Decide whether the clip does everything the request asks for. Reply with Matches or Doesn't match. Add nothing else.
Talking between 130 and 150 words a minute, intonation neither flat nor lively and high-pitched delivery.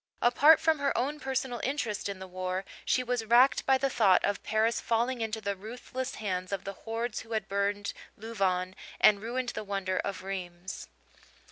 Doesn't match